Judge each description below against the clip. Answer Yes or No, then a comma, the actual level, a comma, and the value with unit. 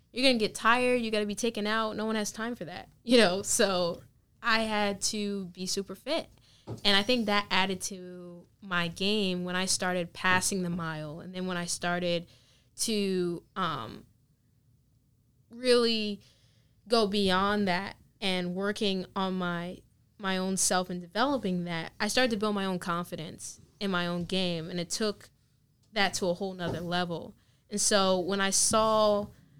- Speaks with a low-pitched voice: No, medium, 185 Hz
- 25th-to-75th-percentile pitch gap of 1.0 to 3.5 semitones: Yes, average, 3.2 semitones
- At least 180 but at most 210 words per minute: No, average, 170 wpm